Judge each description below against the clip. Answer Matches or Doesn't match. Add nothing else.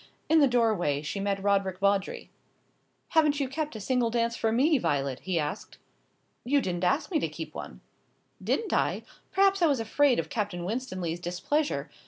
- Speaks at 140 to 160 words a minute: Doesn't match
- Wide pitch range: Matches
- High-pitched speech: Matches